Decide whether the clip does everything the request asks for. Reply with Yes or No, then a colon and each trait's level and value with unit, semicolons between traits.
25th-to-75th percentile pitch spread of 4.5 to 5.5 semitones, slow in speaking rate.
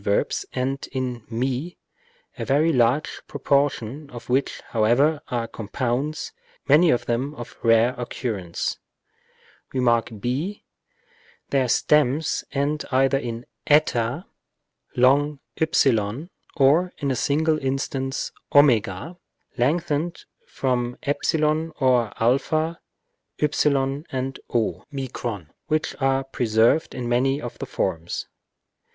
No: average, 3.4 semitones; slow, 105 wpm